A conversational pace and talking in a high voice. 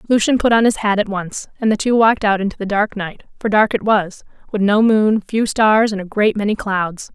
No: fast, 250 wpm; high, 210 Hz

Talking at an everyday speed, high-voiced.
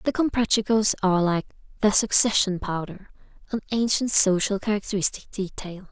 No: slow, 120 wpm; high, 205 Hz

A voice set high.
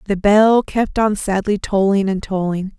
Yes: high, 200 Hz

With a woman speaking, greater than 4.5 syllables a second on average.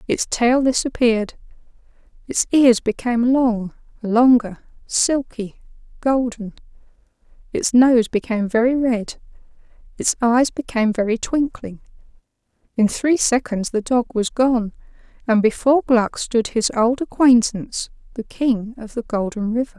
No: female; 4.4 syllables/s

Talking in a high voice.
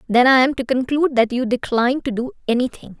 Yes: very high, 250 Hz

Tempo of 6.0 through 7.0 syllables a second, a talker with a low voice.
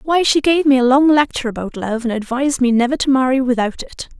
No: 6.2 syllables/s; very high, 260 Hz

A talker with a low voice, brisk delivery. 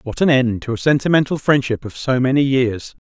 Yes: low, 130 Hz; fast, 215 wpm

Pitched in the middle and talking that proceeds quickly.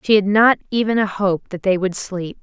No: high, 200 Hz; fast, 245 wpm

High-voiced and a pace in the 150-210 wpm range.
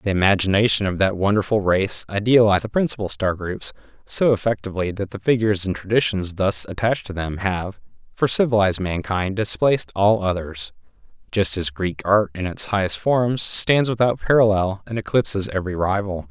No: low, 100 Hz; average, 160 wpm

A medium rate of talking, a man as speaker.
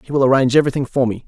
No: fast, 280 wpm; male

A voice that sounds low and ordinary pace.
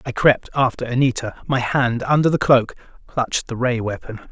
Yes: low, 125 Hz; average, 180 wpm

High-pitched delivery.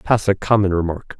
No: low, 100 Hz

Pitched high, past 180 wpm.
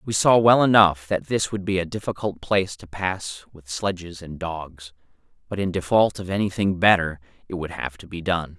No: very low, 90 Hz; fast, 205 wpm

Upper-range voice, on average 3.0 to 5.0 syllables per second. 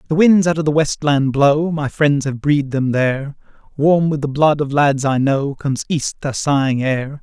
No: medium, 145 Hz; 4.8 syllables/s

